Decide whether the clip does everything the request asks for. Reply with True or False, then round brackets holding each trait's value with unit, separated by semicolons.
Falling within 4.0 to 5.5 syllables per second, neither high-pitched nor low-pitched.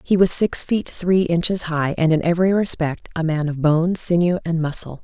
True (5.0 syllables/s; 170 Hz)